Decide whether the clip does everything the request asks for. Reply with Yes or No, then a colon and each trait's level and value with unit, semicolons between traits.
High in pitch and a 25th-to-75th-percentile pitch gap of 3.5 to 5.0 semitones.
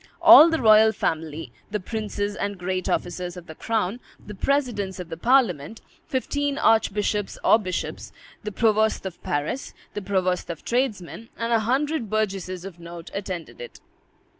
Yes: high, 205 Hz; average, 4.1 semitones